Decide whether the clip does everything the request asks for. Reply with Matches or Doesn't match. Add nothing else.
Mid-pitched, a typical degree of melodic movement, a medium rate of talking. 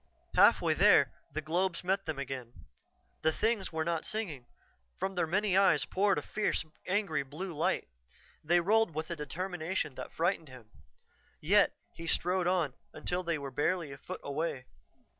Matches